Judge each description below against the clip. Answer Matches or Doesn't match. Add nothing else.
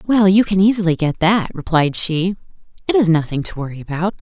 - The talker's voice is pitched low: Doesn't match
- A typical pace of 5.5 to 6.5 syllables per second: Matches